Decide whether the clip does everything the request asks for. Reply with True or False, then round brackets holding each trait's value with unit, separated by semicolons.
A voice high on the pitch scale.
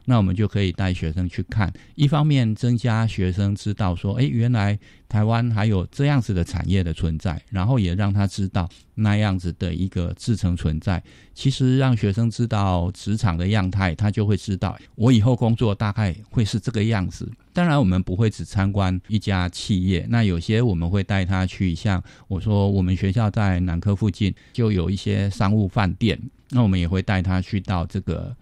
False (100 Hz)